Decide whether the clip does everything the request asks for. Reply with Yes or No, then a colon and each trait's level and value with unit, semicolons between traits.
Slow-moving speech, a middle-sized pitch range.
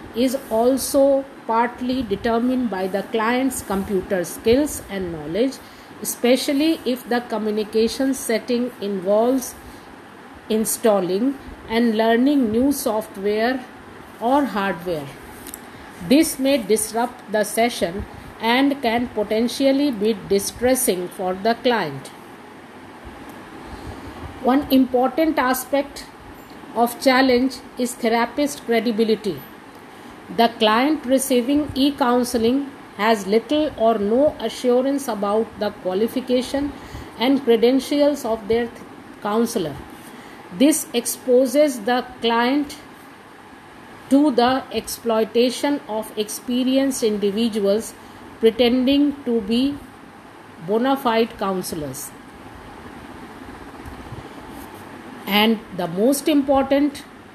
Yes: slow, 90 wpm; average, 3.6 semitones